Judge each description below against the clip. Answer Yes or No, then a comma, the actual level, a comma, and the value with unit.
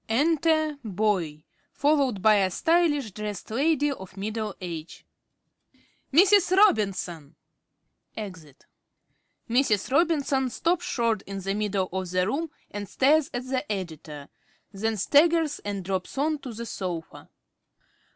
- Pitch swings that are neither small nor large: No, wide, 7.5 semitones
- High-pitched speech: Yes, high, 220 Hz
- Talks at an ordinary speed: No, slow, 125 wpm